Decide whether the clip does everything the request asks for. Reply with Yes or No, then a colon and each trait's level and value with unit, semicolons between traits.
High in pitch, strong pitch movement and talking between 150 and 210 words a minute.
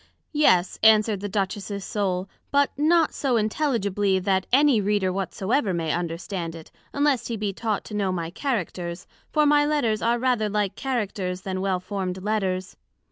No: high, 205 Hz; average, 4.3 semitones; average, 160 wpm